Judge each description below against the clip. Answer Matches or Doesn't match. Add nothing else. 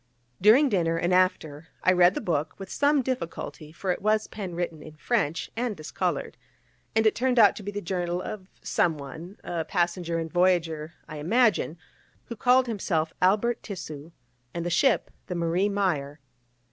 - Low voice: Doesn't match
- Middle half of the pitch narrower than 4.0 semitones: Doesn't match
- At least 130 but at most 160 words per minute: Doesn't match